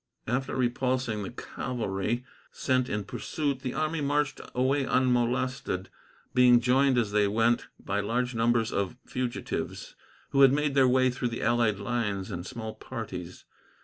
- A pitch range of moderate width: Yes, average, 3.0 semitones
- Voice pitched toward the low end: Yes, low, 125 Hz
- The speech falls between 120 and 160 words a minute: Yes, average, 150 wpm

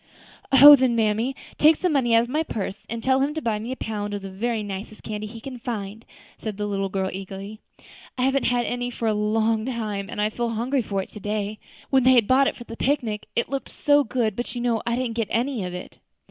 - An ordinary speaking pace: No, fast, 245 wpm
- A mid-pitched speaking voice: No, high, 230 Hz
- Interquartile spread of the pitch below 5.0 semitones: Yes, average, 3.4 semitones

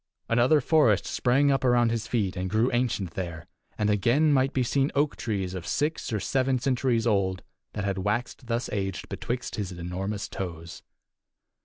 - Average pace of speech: Yes, average, 170 wpm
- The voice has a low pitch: Yes, low, 115 Hz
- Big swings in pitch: No, average, 4.9 semitones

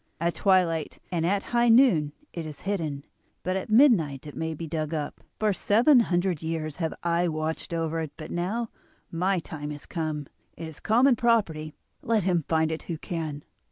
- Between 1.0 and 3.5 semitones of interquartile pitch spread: No, average, 4.0 semitones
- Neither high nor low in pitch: Yes, medium, 165 Hz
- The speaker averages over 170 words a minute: Yes, average, 185 wpm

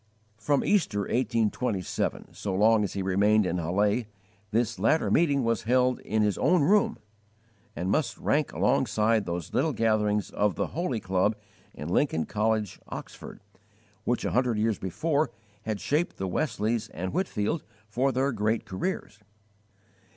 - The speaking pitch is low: Yes, low, 110 Hz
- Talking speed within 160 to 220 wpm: No, average, 145 wpm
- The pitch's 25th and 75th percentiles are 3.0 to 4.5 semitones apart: Yes, average, 4.2 semitones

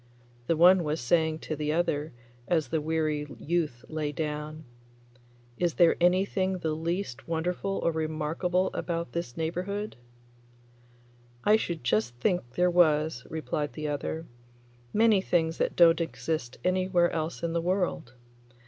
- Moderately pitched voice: Yes, medium, 165 Hz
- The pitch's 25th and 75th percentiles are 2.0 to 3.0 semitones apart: Yes, narrow, 2.6 semitones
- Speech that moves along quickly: No, average, 140 wpm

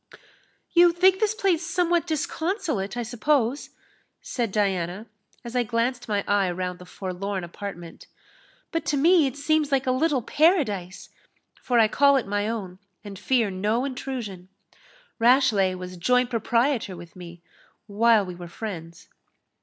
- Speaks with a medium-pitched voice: No, high, 230 Hz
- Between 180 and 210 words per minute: No, average, 145 wpm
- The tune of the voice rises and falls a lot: Yes, wide, 6.7 semitones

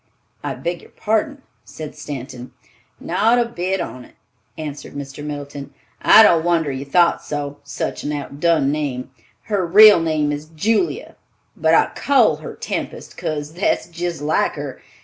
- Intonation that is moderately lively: Yes, average, 3.6 semitones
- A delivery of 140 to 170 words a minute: Yes, average, 150 wpm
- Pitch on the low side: No, medium, 155 Hz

